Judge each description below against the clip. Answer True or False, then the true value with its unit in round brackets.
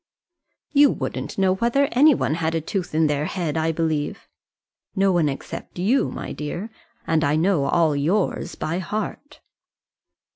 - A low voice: False (170 Hz)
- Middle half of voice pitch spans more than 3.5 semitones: True (4.4 semitones)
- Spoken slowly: False (155 wpm)